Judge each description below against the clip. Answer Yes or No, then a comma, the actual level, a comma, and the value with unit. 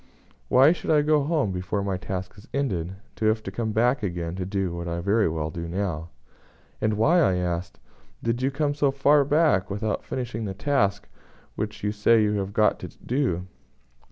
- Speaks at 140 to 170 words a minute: No, average, 200 wpm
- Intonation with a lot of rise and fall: Yes, wide, 6.5 semitones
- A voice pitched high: No, low, 105 Hz